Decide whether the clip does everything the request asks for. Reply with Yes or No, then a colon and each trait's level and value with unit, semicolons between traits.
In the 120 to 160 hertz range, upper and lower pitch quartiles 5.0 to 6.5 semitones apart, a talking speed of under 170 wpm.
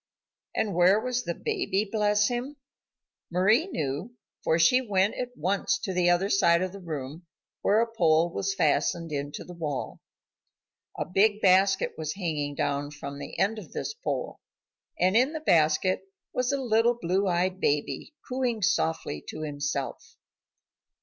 No: high, 190 Hz; wide, 5.4 semitones; average, 155 wpm